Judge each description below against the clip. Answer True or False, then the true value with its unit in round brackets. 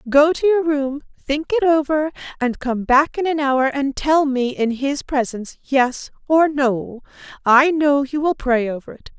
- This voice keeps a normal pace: True (190 wpm)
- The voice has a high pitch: True (280 Hz)